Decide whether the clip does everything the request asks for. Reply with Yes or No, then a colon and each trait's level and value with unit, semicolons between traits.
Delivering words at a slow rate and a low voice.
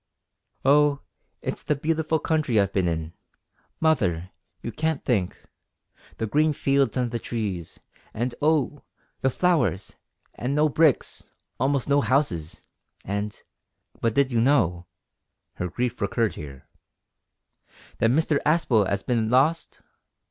Yes: slow, 125 wpm; low, 125 Hz